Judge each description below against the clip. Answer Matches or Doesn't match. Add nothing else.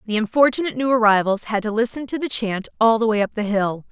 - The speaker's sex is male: Doesn't match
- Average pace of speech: Doesn't match